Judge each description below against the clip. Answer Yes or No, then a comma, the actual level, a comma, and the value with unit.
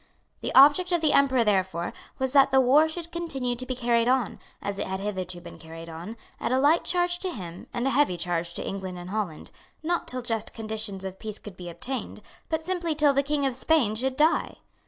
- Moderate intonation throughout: No, wide, 7.3 semitones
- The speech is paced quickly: Yes, fast, 220 wpm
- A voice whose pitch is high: Yes, high, 245 Hz